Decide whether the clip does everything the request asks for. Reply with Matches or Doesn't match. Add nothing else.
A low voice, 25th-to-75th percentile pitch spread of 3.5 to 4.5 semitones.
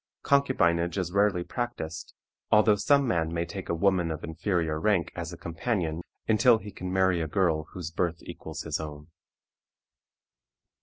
Matches